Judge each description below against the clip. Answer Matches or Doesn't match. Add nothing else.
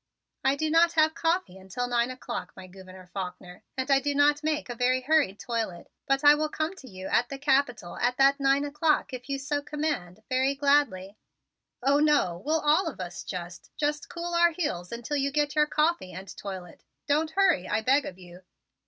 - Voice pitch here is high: Matches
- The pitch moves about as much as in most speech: Doesn't match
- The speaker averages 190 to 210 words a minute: Matches